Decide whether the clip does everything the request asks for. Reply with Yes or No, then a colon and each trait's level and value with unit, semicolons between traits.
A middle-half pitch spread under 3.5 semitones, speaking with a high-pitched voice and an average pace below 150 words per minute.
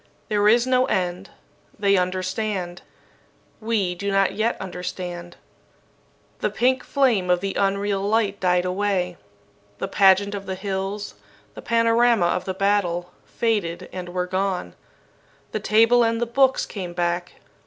Yes: average, 3.1 semitones; high, 195 Hz; average, 140 wpm